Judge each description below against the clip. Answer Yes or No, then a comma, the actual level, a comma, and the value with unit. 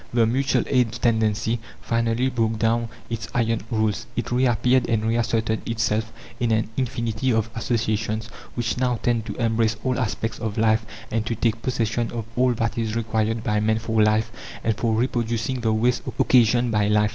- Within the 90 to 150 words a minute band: No, average, 175 wpm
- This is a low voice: Yes, low, 115 Hz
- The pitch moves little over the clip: Yes, narrow, 1.4 semitones